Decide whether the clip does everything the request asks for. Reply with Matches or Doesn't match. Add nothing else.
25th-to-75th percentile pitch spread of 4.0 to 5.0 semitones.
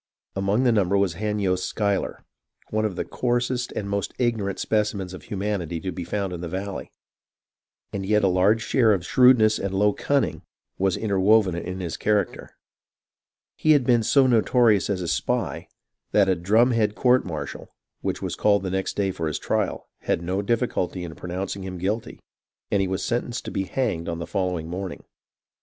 Doesn't match